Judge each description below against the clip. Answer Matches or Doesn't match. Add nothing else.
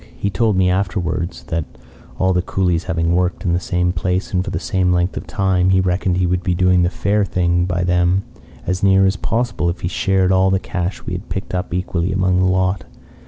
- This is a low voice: Matches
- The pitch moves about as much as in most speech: Doesn't match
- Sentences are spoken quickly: Matches